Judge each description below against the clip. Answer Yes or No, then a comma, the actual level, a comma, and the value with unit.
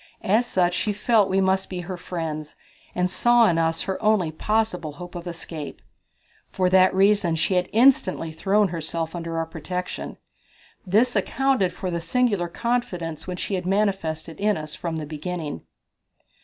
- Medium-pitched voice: Yes, medium, 180 Hz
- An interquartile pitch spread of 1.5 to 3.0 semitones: No, average, 3.7 semitones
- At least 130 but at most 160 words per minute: No, average, 170 wpm